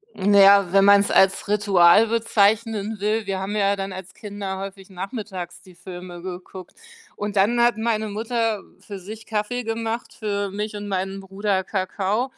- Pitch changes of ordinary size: No, narrow, 2.1 semitones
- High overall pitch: Yes, high, 200 Hz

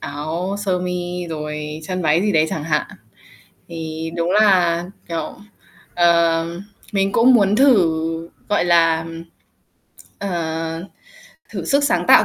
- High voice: No, medium, 170 Hz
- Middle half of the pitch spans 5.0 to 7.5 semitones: No, average, 2.9 semitones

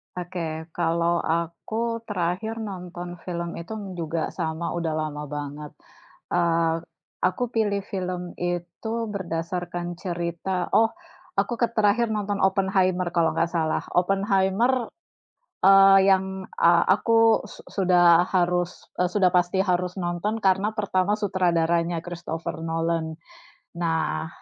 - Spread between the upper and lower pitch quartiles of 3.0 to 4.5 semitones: No, narrow, 2.5 semitones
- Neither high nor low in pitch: Yes, medium, 180 Hz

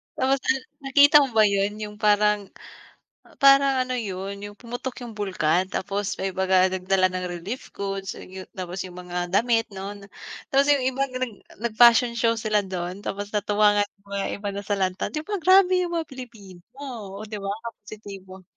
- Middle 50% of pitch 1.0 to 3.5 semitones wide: No, average, 4.3 semitones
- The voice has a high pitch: Yes, high, 205 Hz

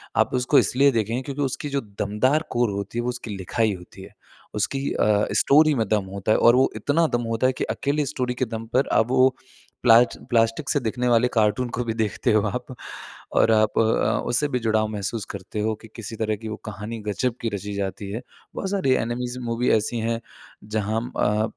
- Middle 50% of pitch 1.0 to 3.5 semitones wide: Yes, average, 2.9 semitones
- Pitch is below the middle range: Yes, low, 115 Hz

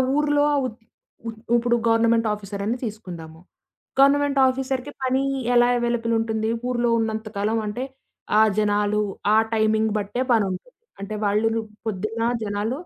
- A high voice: Yes, high, 225 Hz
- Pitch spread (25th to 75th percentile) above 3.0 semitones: No, average, 2.7 semitones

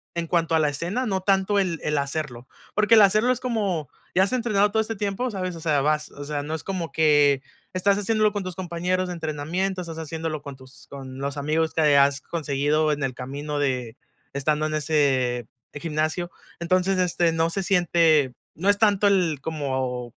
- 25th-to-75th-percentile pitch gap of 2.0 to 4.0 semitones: No, average, 4.7 semitones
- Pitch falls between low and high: Yes, medium, 160 Hz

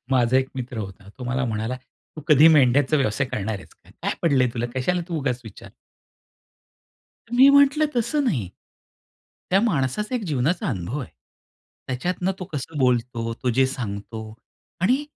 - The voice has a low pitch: Yes, low, 130 Hz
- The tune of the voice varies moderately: No, wide, 6.6 semitones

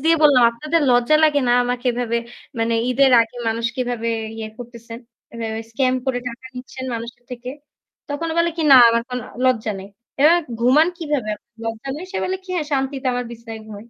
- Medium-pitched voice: No, high, 245 Hz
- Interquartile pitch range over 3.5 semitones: No, average, 3.0 semitones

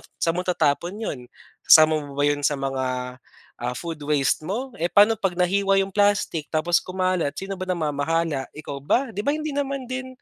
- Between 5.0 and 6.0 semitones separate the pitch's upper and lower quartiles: Yes, wide, 5.6 semitones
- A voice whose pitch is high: No, medium, 170 Hz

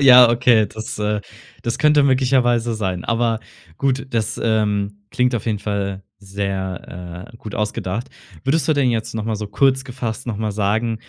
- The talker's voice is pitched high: No, low, 110 Hz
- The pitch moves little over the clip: No, average, 3.4 semitones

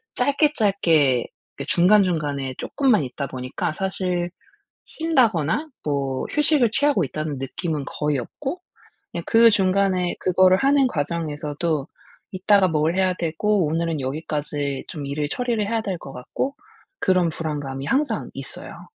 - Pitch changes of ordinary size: No, wide, 6.2 semitones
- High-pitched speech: No, medium, 175 Hz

